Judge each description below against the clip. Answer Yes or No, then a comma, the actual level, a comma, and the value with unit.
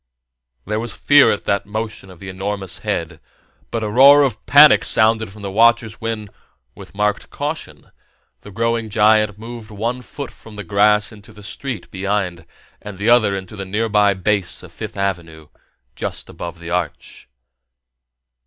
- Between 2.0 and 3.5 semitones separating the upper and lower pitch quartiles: Yes, average, 2.8 semitones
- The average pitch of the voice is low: Yes, low, 105 Hz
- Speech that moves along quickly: No, average, 160 wpm